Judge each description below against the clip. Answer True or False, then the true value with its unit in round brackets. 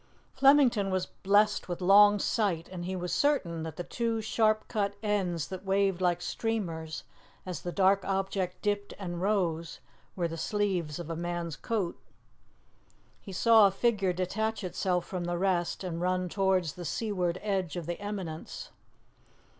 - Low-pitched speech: False (185 Hz)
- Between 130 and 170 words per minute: True (160 wpm)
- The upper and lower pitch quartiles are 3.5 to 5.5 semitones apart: False (2.9 semitones)